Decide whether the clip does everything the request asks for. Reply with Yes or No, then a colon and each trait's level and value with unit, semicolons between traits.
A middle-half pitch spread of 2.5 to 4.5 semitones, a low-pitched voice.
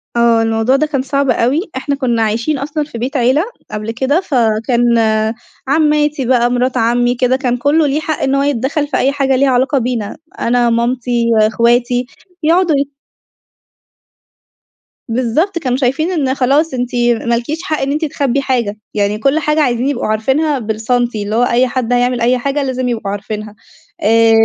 No: average, 3.1 semitones; very high, 255 Hz